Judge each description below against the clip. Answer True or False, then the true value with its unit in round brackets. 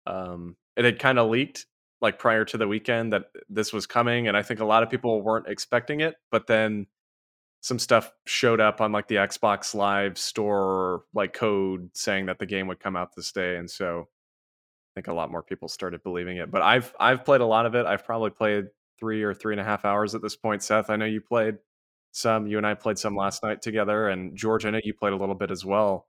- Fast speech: True (240 wpm)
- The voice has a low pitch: True (105 Hz)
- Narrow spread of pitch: True (2.3 semitones)